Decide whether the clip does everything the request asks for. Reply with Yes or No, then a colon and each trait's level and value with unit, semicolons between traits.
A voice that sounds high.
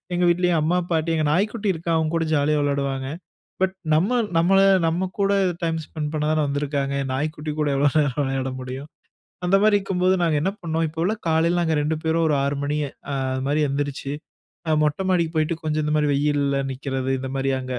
No: medium, 155 Hz